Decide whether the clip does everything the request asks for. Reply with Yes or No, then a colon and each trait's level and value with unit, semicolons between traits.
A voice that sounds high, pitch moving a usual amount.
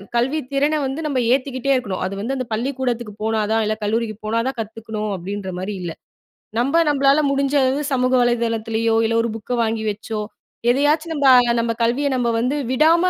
Yes: high, 240 Hz; average, 3.7 semitones